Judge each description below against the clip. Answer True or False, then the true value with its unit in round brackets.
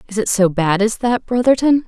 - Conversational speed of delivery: False (225 wpm)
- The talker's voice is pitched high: True (220 Hz)